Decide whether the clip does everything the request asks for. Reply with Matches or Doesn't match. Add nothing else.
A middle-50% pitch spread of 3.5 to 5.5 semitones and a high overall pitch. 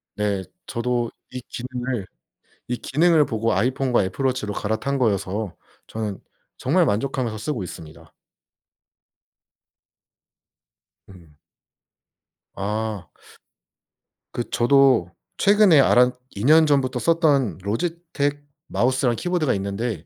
Doesn't match